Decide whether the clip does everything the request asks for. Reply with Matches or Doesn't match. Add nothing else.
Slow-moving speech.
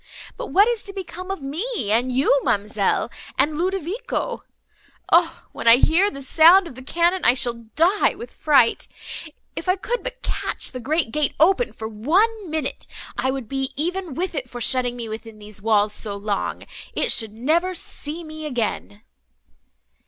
Doesn't match